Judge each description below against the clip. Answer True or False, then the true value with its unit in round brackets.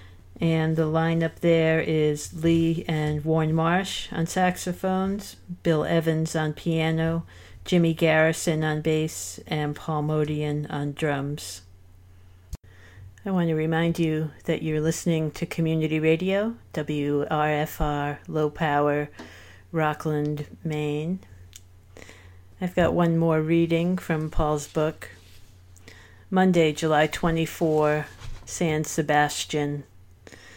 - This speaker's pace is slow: True (105 wpm)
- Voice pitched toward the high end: False (155 Hz)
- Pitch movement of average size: False (2.2 semitones)